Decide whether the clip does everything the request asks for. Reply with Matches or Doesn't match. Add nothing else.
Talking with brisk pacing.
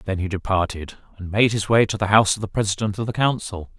Matches